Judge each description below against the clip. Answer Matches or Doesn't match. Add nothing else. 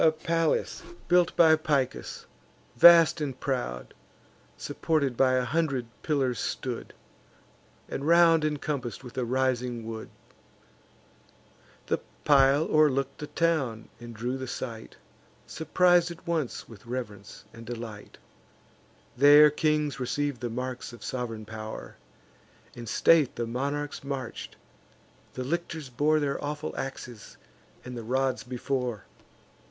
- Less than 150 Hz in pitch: Matches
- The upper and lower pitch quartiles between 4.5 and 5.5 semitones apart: Doesn't match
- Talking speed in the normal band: Doesn't match